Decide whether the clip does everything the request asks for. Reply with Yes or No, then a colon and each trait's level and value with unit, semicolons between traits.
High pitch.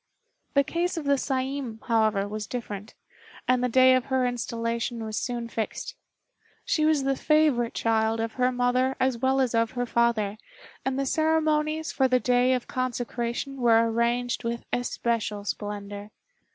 Yes: high, 245 Hz